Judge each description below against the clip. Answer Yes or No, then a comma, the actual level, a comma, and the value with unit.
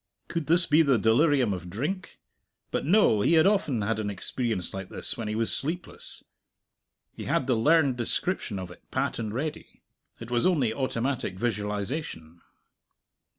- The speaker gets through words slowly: No, average, 160 wpm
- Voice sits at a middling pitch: No, low, 120 Hz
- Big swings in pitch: Yes, wide, 6.4 semitones